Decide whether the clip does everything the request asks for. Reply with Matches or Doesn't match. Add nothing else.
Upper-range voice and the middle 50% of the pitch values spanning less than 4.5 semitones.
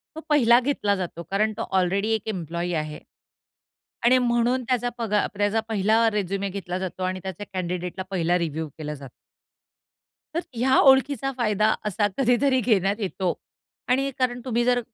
Doesn't match